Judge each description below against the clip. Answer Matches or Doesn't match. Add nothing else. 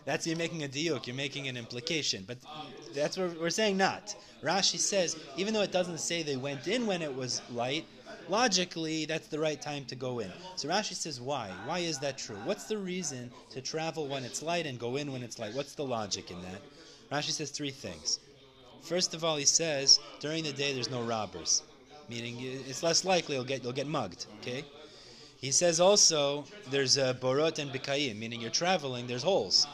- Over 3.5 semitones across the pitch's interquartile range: Matches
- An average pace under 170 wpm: Doesn't match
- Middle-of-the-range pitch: Matches